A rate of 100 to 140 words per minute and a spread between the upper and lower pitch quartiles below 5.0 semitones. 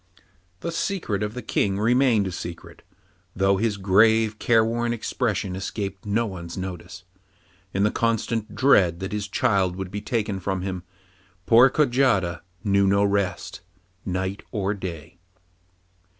Yes: slow, 135 wpm; average, 3.1 semitones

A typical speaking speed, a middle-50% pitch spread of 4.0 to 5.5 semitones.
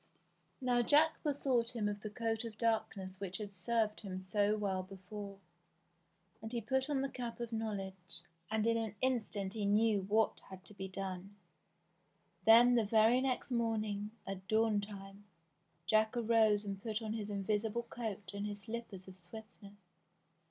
No: average, 165 wpm; narrow, 2.5 semitones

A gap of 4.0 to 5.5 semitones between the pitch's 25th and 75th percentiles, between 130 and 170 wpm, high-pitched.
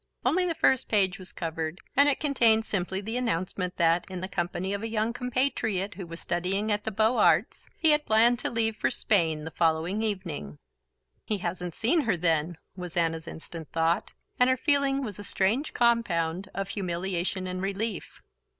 No: average, 4.7 semitones; average, 185 wpm; high, 195 Hz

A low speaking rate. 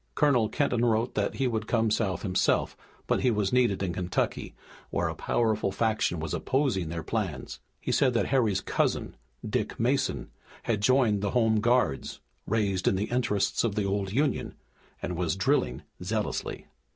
No: average, 165 wpm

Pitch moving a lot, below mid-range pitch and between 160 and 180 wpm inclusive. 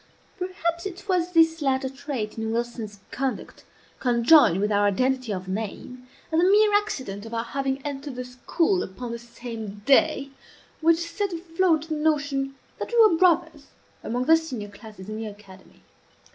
No: wide, 6.6 semitones; very high, 270 Hz; average, 165 wpm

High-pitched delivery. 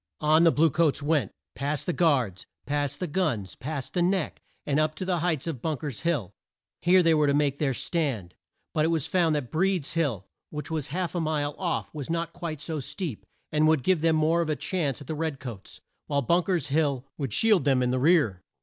No: medium, 155 Hz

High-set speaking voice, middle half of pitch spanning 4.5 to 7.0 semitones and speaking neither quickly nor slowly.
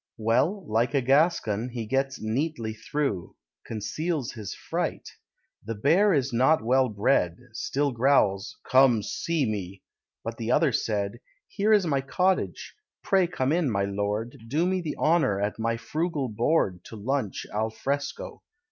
No: low, 125 Hz; wide, 5.5 semitones; average, 150 wpm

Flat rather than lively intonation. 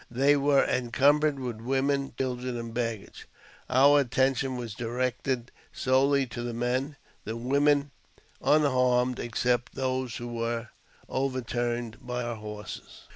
Yes: narrow, 2.3 semitones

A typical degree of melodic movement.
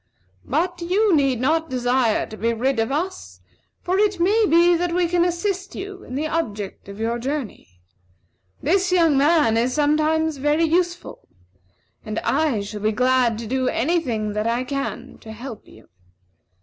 No: wide, 6.7 semitones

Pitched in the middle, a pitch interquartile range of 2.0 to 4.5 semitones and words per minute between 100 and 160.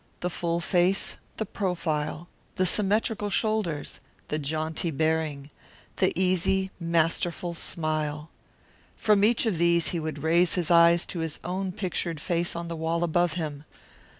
Yes: medium, 170 Hz; narrow, 2.5 semitones; average, 145 wpm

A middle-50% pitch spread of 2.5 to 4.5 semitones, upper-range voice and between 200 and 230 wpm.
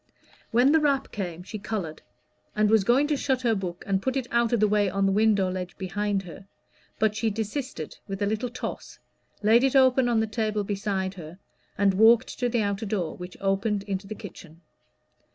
Yes: average, 3.4 semitones; high, 210 Hz; fast, 205 wpm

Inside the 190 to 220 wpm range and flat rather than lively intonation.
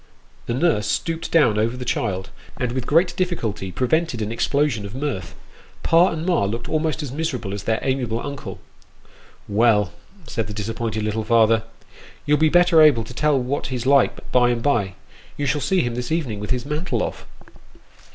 No: average, 195 wpm; average, 5.3 semitones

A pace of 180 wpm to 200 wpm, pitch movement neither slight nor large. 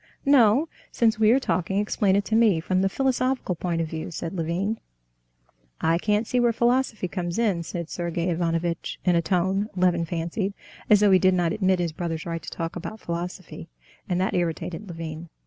Yes: average, 190 wpm; average, 3.8 semitones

